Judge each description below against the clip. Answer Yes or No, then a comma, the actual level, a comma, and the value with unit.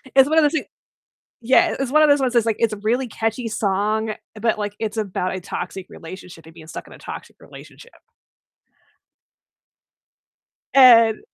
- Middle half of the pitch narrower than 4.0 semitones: No, average, 4.3 semitones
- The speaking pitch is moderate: No, high, 220 Hz